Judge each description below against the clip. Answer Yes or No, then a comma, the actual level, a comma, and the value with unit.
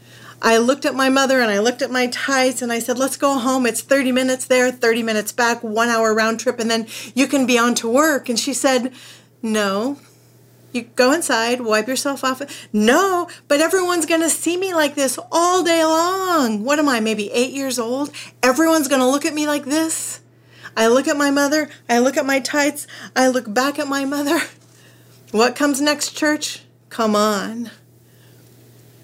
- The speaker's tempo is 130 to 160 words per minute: No, average, 195 wpm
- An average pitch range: Yes, average, 3.8 semitones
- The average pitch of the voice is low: No, very high, 265 Hz